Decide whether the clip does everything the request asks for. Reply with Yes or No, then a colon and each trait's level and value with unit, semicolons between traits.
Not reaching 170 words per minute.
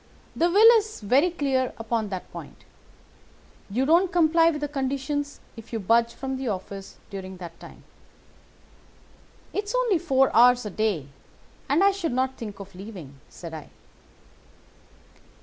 Yes: average, 150 wpm